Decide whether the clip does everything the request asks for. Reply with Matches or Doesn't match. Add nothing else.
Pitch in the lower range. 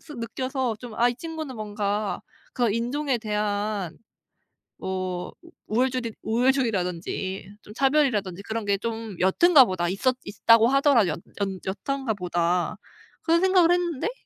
Doesn't match